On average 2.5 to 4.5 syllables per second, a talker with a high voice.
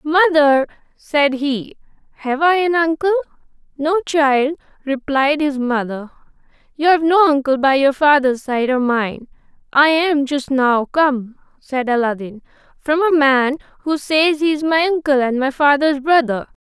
Yes: 4.3 syllables/s; very high, 285 Hz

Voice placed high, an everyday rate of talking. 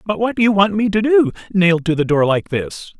No: high, 195 Hz; fast, 280 wpm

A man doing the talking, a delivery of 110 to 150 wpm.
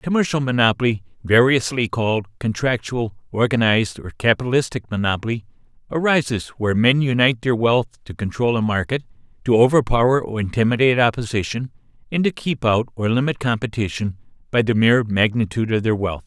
Yes: male; average, 140 wpm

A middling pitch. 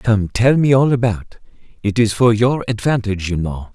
No: low, 110 Hz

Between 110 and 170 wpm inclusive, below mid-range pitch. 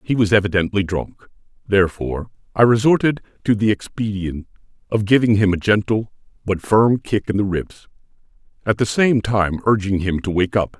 Yes: average, 165 wpm; low, 105 Hz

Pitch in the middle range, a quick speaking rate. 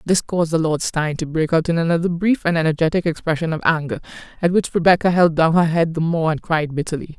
Yes: medium, 165 Hz; fast, 235 wpm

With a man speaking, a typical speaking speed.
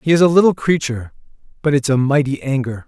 No: male; fast, 210 wpm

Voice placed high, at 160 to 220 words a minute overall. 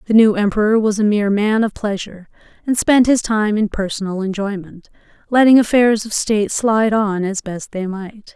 Yes: high, 210 Hz; average, 185 wpm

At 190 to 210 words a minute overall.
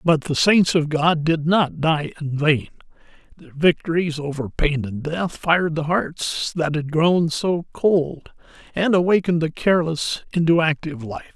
No: average, 165 wpm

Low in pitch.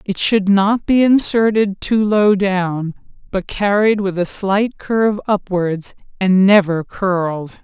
No: high, 195 Hz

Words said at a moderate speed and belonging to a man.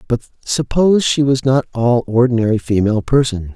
Yes: average, 150 wpm; male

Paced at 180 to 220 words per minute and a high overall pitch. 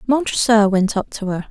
Yes: average, 200 wpm; high, 215 Hz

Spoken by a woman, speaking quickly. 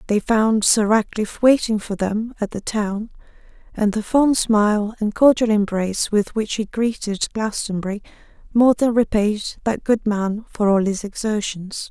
No: female; average, 160 wpm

